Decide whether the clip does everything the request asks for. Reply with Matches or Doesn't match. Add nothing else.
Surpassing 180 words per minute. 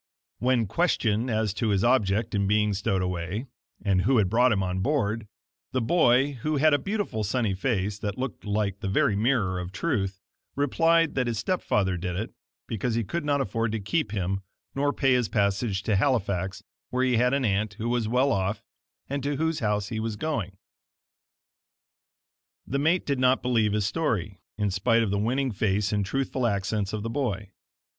Matches